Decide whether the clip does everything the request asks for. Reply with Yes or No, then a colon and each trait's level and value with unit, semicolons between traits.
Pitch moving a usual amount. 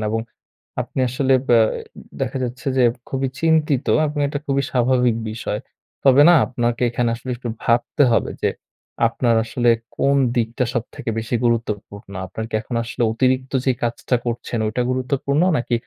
No: narrow, 2.3 semitones